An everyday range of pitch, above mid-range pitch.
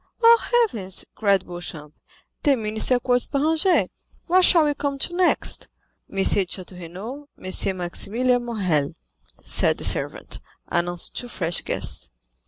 No: wide, 8.0 semitones; high, 225 Hz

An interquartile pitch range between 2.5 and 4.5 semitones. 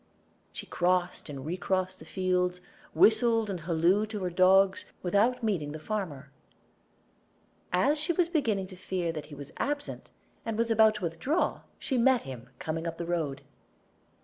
No: average, 4.9 semitones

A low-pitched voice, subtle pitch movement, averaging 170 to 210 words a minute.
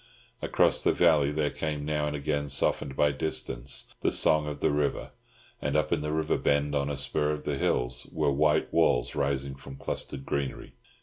Yes: very low, 75 Hz; narrow, 1.6 semitones; average, 190 wpm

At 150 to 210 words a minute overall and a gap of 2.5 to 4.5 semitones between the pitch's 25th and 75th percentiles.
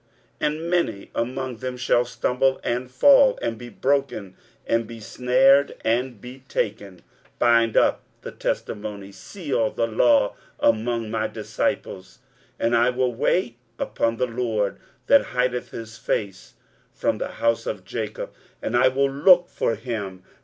Yes: average, 155 wpm; average, 2.8 semitones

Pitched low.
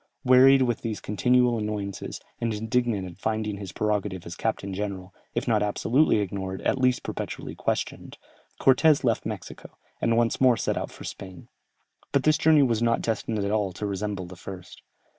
Yes: low, 110 Hz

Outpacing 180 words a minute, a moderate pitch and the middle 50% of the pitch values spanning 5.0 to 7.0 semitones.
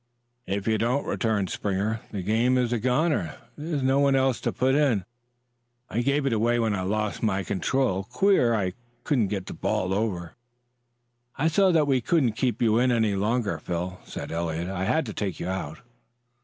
No: average, 190 wpm; low, 110 Hz; average, 5.3 semitones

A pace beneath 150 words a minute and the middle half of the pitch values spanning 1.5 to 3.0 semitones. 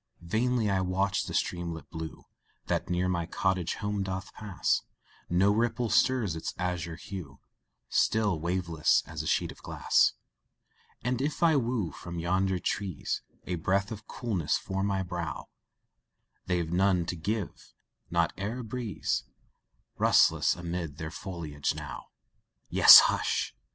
No: average, 140 wpm; average, 3.4 semitones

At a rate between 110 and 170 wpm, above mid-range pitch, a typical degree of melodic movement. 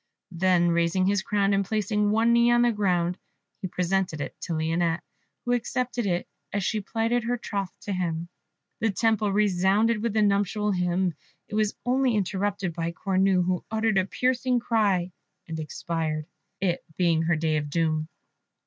Yes: average, 165 wpm; high, 195 Hz; average, 3.9 semitones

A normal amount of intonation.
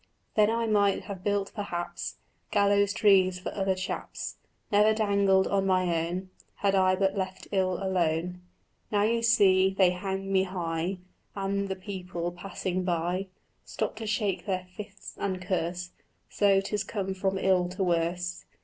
No: narrow, 1.8 semitones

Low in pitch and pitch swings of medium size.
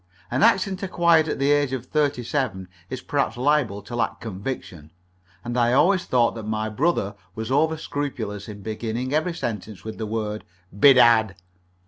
Yes: low, 120 Hz; average, 5.0 semitones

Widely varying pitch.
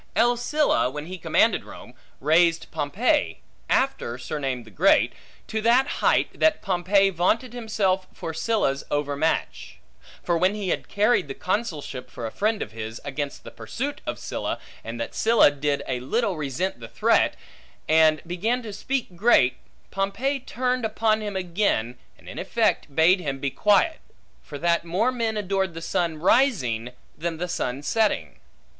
Yes: wide, 7.3 semitones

